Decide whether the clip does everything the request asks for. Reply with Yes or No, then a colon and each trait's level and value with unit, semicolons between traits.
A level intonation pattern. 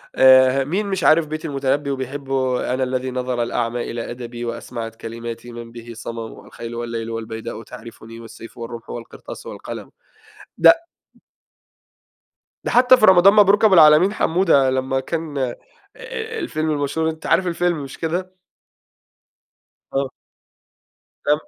No: wide, 5.4 semitones